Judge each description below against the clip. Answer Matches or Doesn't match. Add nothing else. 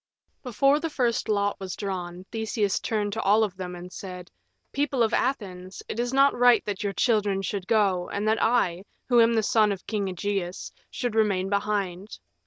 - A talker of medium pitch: Doesn't match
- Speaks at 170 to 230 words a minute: Matches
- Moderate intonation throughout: Matches